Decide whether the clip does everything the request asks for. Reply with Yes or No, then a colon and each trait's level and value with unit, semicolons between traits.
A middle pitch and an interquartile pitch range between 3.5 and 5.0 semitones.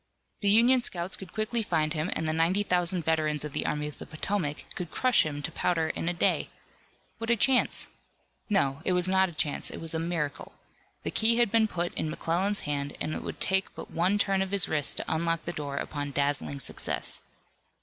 Yes: medium, 170 Hz; average, 4.3 semitones